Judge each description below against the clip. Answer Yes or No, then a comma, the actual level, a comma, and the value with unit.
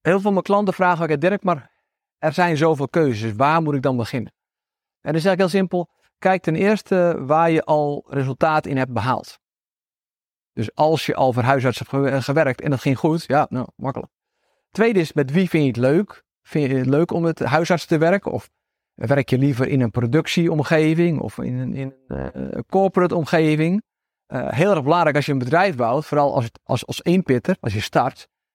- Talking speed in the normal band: No, fast, 205 wpm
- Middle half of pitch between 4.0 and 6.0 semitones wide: Yes, average, 4.4 semitones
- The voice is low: No, medium, 155 Hz